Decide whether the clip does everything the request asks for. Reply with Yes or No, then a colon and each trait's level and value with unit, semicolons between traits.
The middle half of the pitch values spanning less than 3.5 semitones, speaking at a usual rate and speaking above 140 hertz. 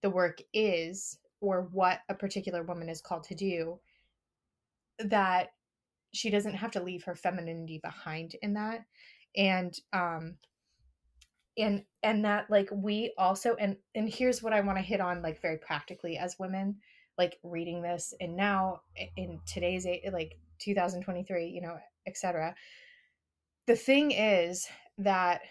Yes: average, 2.9 semitones; average, 145 wpm; medium, 185 Hz